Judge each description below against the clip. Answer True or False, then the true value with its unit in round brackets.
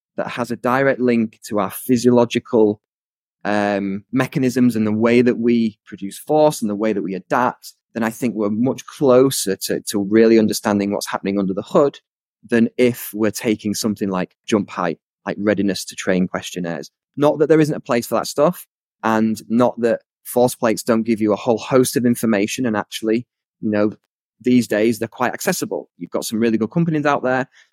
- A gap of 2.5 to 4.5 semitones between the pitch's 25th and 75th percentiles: True (3.0 semitones)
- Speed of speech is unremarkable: True (195 wpm)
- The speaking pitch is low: True (115 Hz)